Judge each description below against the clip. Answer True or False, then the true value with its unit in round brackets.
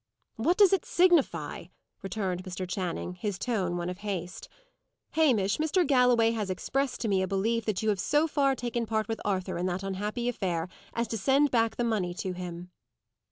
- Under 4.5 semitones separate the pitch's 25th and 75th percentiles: False (5.0 semitones)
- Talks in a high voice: True (210 Hz)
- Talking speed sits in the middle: True (190 wpm)